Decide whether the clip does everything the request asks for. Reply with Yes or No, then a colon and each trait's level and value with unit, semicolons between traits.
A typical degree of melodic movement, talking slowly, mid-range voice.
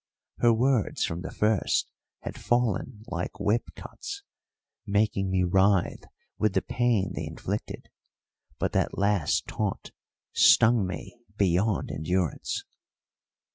No: average, 3.6 semitones; slow, 115 wpm; low, 100 Hz